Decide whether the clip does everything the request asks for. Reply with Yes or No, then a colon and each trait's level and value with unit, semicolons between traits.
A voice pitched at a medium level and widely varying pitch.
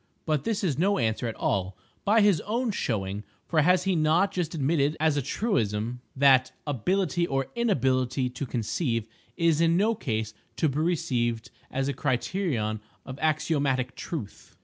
Yes: medium, 145 Hz; wide, 6.1 semitones